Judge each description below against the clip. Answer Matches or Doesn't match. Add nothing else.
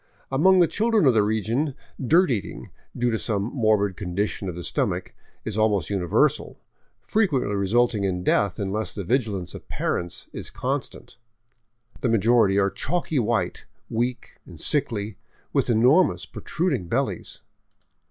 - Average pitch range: Matches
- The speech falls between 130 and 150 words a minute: Matches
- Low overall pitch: Matches